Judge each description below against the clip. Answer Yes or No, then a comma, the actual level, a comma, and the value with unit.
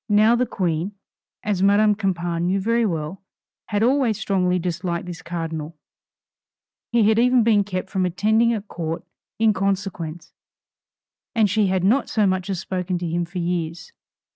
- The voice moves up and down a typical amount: Yes, average, 3.6 semitones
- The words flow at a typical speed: Yes, average, 160 wpm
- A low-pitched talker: No, high, 190 Hz